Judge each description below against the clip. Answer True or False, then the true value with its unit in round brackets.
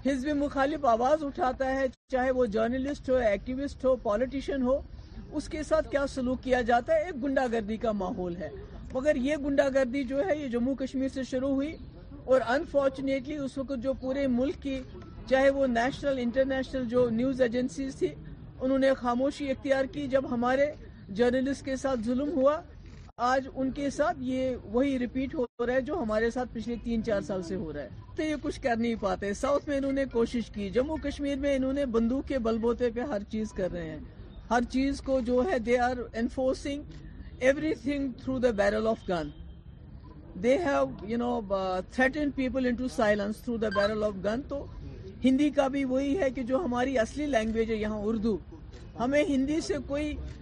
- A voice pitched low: False (260 Hz)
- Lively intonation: False (2.7 semitones)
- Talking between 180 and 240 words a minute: True (185 wpm)